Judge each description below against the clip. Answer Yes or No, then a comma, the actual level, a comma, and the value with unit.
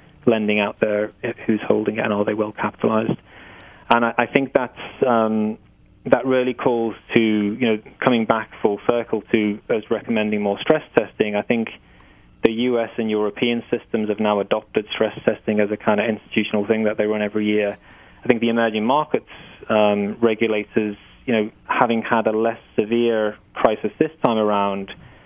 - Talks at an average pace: Yes, average, 175 wpm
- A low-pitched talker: Yes, low, 110 Hz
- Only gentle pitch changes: Yes, narrow, 1.7 semitones